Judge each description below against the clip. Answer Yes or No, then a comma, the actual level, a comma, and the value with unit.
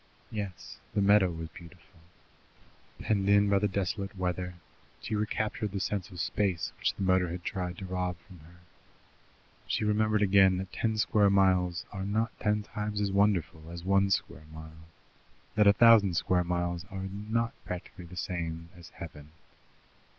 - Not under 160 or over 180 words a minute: Yes, average, 165 wpm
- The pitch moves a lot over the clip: No, average, 2.7 semitones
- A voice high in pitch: No, very low, 95 Hz